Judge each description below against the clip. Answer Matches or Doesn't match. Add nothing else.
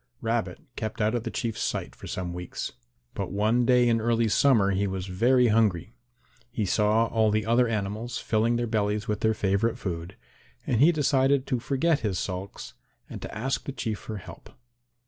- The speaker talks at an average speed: Matches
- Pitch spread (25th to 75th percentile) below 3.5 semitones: Matches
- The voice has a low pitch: Matches